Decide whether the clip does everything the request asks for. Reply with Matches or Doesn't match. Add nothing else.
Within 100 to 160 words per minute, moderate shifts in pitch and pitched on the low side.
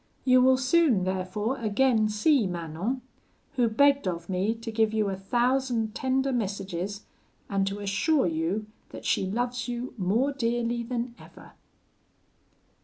Doesn't match